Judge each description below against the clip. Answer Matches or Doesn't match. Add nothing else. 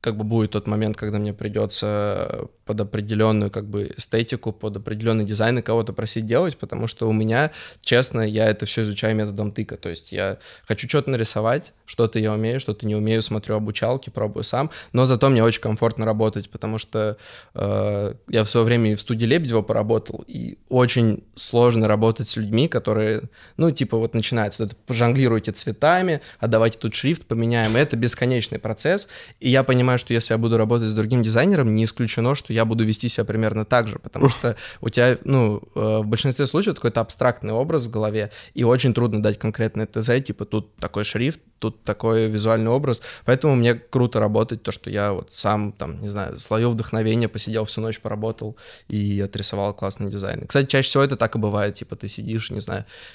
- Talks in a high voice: Doesn't match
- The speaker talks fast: Matches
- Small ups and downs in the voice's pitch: Matches